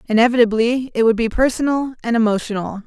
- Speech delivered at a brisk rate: No, average, 145 wpm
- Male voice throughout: No, female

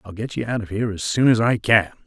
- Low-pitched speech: Yes, low, 110 Hz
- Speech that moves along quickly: Yes, fast, 320 wpm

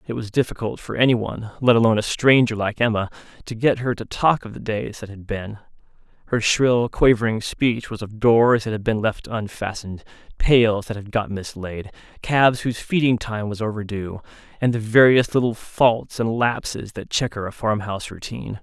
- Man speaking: Yes, male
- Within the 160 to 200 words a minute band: Yes, average, 185 wpm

